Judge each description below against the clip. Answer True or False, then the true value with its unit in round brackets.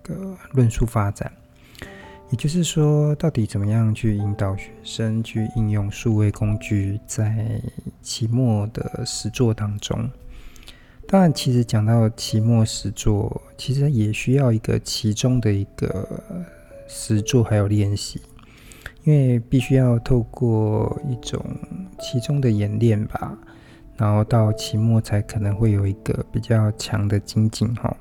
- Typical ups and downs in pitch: True (3.2 semitones)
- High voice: False (115 Hz)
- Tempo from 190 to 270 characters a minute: True (205 characters per minute)